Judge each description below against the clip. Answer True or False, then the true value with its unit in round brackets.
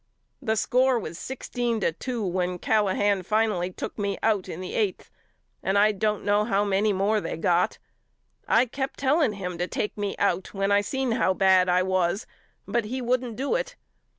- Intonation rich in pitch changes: False (3.8 semitones)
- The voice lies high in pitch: True (205 Hz)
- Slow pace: False (185 wpm)